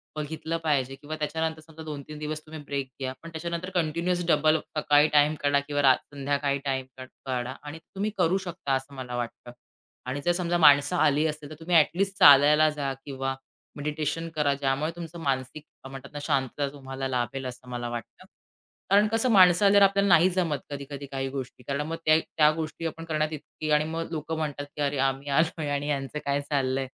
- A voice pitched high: No, medium, 150 Hz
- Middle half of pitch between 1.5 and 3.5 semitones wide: Yes, average, 2.8 semitones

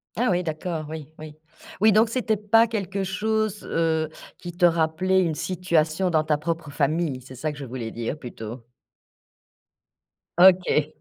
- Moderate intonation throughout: Yes, average, 3.8 semitones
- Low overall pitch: No, medium, 165 Hz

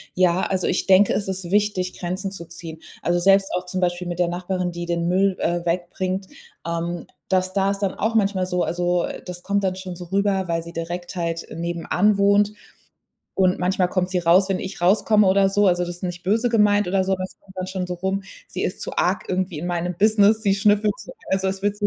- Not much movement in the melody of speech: Yes, narrow, 2.0 semitones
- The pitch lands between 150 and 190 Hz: Yes, medium, 185 Hz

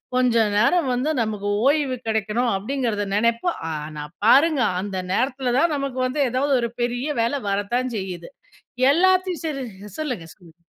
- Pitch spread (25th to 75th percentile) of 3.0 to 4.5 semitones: No, average, 5.1 semitones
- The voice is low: No, high, 245 Hz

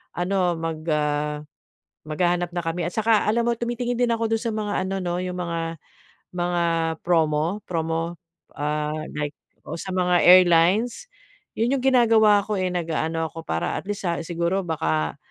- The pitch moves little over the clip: No, average, 4.1 semitones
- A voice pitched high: No, medium, 175 Hz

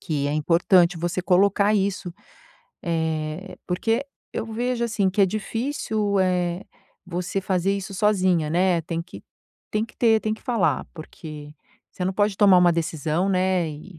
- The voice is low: No, medium, 185 Hz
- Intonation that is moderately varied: Yes, average, 3.2 semitones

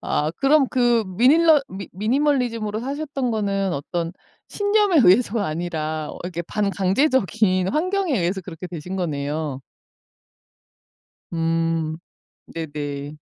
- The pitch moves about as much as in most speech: No, wide, 7.5 semitones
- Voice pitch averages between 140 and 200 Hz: Yes, high, 190 Hz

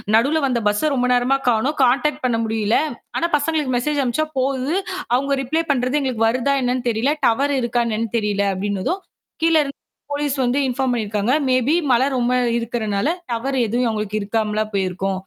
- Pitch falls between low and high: No, high, 245 Hz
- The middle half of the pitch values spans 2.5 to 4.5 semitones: Yes, average, 3.9 semitones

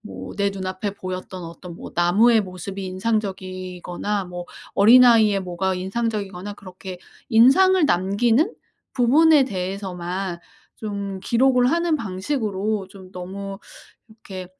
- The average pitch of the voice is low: No, high, 195 Hz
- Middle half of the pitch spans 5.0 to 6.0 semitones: No, average, 3.6 semitones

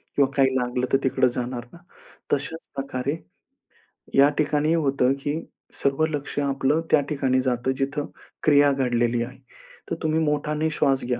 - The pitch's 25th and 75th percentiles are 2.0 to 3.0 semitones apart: Yes, narrow, 2.4 semitones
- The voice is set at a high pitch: No, low, 135 Hz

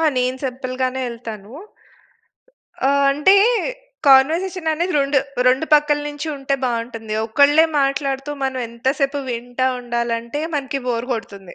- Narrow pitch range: No, average, 3.2 semitones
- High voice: Yes, very high, 265 Hz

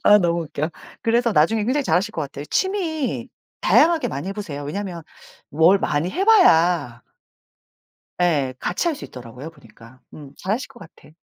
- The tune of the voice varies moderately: No, wide, 8.4 semitones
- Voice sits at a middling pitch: Yes, medium, 175 Hz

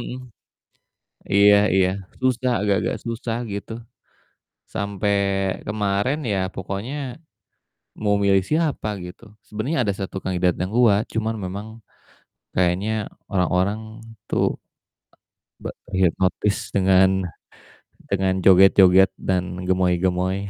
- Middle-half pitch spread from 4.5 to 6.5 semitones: No, average, 2.7 semitones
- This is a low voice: Yes, low, 100 Hz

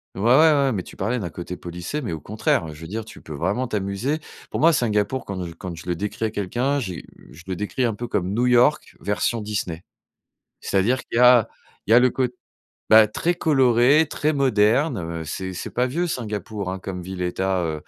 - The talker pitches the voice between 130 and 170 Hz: No, low, 105 Hz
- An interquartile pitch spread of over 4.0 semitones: Yes, wide, 5.5 semitones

